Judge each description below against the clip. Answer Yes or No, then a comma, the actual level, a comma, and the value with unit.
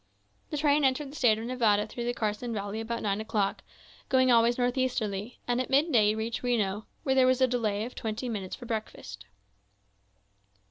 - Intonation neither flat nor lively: Yes, average, 3.1 semitones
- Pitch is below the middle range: No, high, 235 Hz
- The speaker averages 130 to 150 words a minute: No, average, 180 wpm